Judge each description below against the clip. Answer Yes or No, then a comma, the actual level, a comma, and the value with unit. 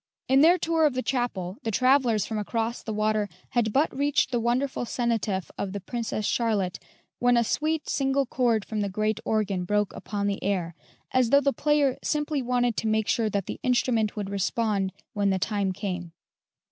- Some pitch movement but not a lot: Yes, average, 4.0 semitones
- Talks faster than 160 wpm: Yes, average, 190 wpm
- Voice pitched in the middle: No, high, 225 Hz